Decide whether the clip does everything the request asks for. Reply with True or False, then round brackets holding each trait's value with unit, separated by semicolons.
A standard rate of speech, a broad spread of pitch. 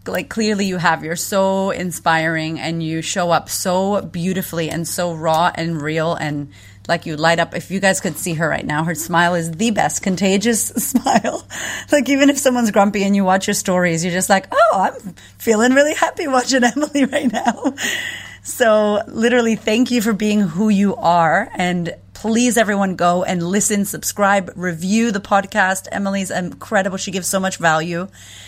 False (180 wpm; 4.2 semitones)